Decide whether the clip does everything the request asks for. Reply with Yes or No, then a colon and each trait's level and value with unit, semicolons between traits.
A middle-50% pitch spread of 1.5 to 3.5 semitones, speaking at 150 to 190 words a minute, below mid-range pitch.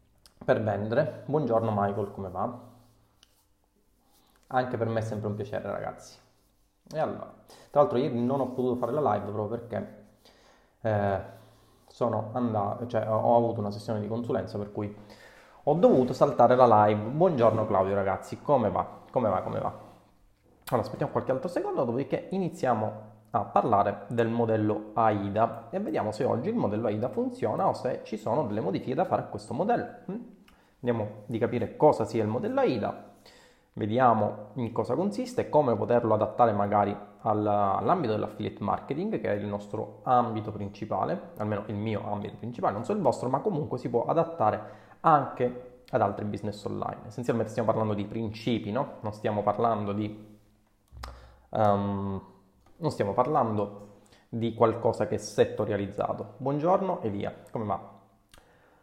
Yes: average, 2.7 semitones; average, 155 wpm; low, 110 Hz